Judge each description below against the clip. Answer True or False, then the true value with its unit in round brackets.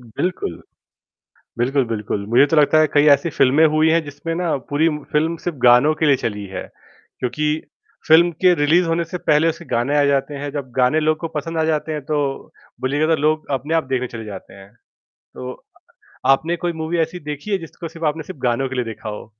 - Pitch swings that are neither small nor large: True (3.7 semitones)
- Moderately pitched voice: True (150 Hz)